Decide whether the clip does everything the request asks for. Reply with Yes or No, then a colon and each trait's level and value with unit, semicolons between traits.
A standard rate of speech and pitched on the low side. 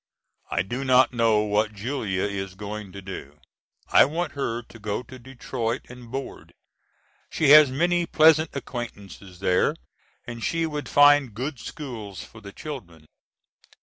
Yes: average, 150 wpm; low, 120 Hz